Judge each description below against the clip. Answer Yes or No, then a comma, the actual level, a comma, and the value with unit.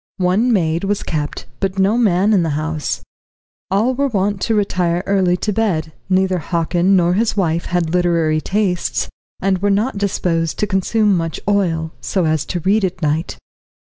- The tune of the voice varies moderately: Yes, average, 3.3 semitones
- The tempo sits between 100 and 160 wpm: No, average, 175 wpm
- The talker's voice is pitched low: No, medium, 185 Hz